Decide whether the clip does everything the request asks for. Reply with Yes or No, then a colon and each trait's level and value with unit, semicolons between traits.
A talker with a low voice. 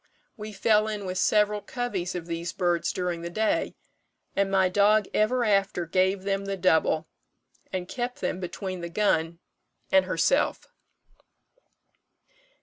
No: high, 190 Hz